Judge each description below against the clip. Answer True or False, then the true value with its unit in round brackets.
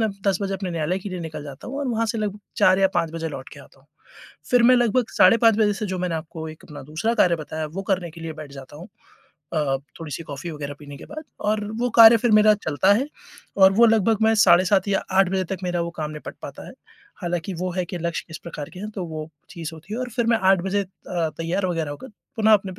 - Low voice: False (185 Hz)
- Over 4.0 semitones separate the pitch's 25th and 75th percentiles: True (4.7 semitones)